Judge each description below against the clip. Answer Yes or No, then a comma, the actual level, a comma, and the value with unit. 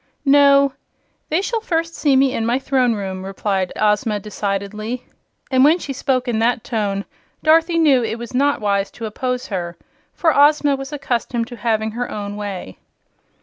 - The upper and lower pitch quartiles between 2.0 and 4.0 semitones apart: No, average, 5.0 semitones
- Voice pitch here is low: No, high, 240 Hz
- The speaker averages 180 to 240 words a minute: No, average, 170 wpm